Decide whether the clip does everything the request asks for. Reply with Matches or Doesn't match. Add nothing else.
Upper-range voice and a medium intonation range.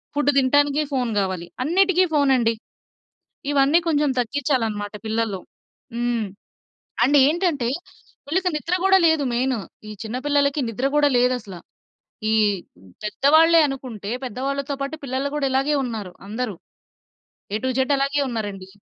Matches